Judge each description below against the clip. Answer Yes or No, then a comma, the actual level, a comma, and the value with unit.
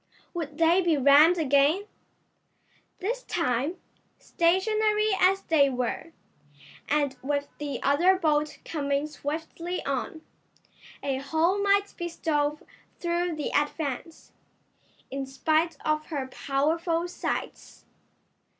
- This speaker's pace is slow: Yes, slow, 105 wpm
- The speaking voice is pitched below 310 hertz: No, very high, 315 Hz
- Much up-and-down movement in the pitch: No, average, 3.5 semitones